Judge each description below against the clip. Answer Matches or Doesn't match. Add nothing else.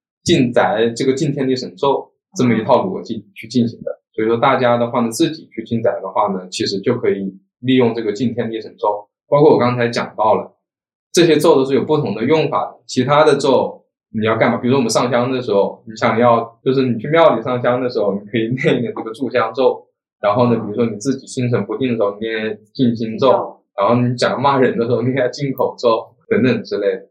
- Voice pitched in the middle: Doesn't match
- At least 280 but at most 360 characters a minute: Matches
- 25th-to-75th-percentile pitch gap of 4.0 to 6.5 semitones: Doesn't match